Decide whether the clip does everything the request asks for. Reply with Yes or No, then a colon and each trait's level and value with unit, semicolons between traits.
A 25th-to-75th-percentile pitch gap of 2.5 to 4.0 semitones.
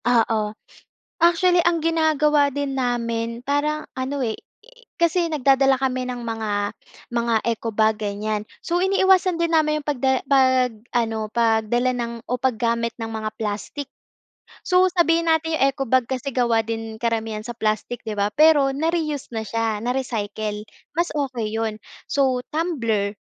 No: average, 4.9 semitones